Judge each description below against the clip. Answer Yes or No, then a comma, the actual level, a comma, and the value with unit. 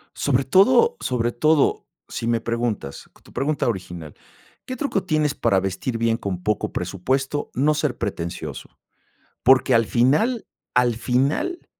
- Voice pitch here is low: Yes, low, 125 Hz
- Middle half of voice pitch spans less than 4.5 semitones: No, average, 5.1 semitones